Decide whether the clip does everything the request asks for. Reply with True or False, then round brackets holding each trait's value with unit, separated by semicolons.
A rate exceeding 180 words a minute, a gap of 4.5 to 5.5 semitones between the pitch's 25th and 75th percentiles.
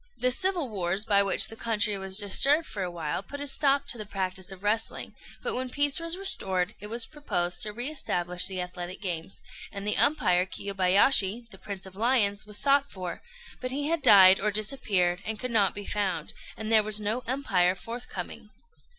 True (200 wpm; 5.0 semitones)